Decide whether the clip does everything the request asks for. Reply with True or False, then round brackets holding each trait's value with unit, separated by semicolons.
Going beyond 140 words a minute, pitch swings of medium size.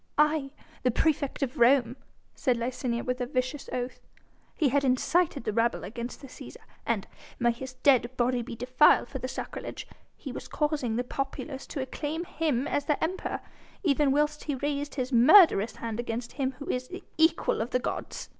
True (185 wpm; 3.2 semitones)